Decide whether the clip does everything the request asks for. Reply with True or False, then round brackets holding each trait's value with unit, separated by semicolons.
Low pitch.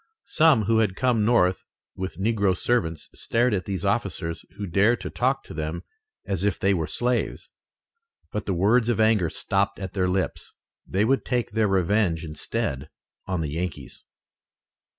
True (100 Hz)